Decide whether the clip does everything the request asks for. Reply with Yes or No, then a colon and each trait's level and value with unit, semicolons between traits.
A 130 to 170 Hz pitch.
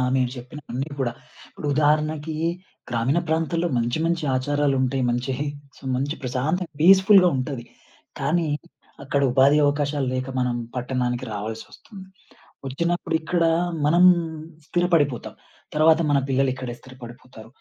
Yes: medium, 140 Hz